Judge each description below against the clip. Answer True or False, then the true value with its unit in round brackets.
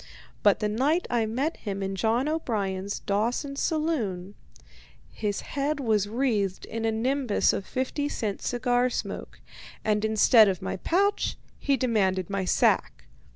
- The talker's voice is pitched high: True (225 Hz)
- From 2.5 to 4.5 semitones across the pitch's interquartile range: False (5.0 semitones)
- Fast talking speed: False (145 wpm)